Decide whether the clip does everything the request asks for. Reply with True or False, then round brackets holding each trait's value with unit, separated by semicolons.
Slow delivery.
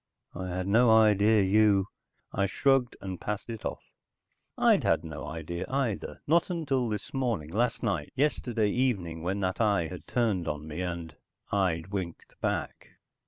False (160 wpm)